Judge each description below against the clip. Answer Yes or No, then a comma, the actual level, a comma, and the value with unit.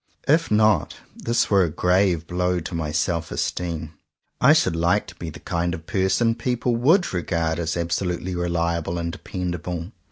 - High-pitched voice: No, very low, 90 Hz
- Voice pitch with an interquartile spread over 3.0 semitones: No, average, 2.7 semitones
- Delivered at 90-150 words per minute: No, average, 165 wpm